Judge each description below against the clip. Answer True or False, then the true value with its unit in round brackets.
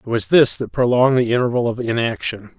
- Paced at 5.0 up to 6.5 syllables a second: True (6.0 syllables/s)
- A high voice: False (120 Hz)